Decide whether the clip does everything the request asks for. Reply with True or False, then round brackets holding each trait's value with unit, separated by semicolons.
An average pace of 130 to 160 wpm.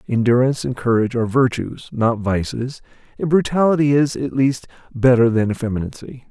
True (145 wpm)